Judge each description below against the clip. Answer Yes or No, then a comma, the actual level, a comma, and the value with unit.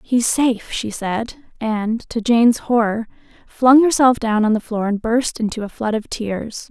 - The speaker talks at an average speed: Yes, average, 180 wpm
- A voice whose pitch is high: Yes, high, 230 Hz